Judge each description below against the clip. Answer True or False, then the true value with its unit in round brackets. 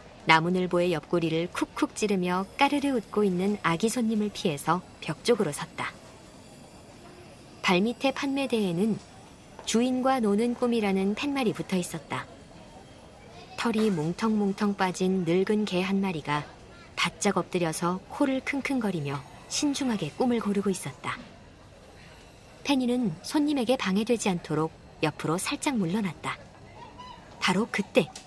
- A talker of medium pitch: False (200 Hz)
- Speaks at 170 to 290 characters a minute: True (270 characters per minute)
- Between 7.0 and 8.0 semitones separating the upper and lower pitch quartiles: False (5.5 semitones)